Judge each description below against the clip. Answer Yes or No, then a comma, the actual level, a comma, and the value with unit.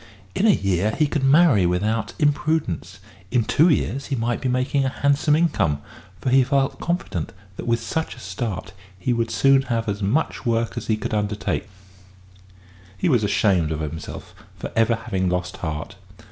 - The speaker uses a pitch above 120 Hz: No, low, 115 Hz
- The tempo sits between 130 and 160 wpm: No, average, 185 wpm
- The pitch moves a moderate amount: No, wide, 5.9 semitones